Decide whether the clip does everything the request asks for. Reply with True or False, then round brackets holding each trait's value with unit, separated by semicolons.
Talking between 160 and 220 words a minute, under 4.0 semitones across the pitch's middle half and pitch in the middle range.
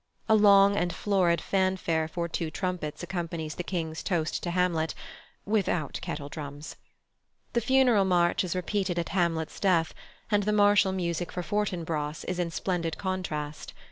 False (145 wpm; 3.0 semitones; 175 Hz)